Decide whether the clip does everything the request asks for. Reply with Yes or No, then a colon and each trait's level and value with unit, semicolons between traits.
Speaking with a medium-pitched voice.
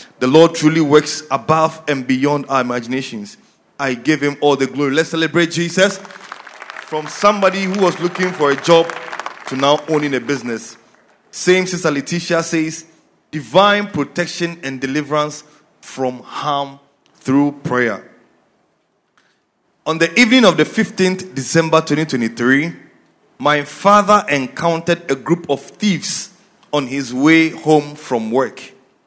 Yes: medium, 155 Hz